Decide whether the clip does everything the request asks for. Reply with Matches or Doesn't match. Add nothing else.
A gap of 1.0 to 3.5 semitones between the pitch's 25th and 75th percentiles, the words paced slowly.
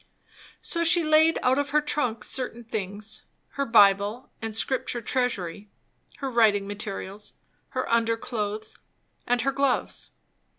Doesn't match